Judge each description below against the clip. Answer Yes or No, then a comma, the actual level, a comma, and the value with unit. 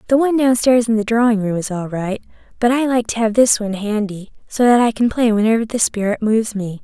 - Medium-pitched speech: No, high, 225 Hz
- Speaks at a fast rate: Yes, fast, 245 wpm